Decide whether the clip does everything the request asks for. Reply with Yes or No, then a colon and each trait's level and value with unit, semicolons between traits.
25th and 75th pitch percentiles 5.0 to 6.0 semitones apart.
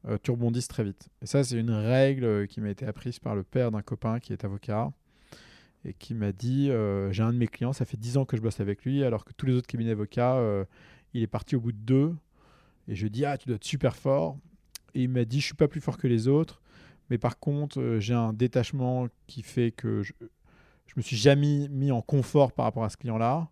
No: average, 3.3 semitones